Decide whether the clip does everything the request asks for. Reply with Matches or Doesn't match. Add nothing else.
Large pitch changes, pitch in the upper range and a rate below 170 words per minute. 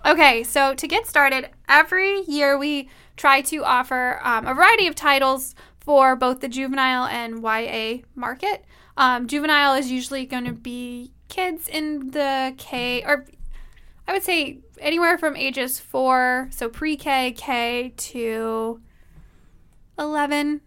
Doesn't match